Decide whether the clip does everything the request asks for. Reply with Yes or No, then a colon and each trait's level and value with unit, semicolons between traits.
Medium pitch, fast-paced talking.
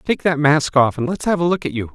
Yes: medium, 150 Hz; fast, 340 wpm